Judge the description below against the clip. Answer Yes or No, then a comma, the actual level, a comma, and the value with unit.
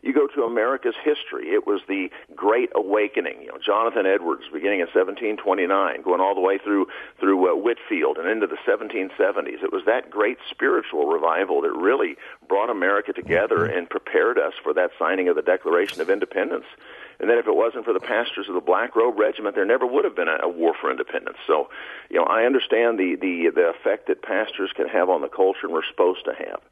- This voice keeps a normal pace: No, fast, 215 wpm